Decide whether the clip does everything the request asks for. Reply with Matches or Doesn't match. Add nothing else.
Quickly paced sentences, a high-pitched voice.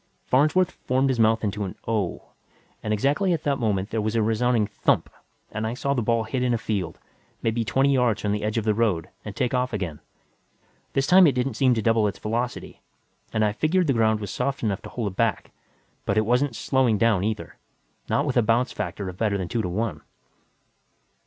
Doesn't match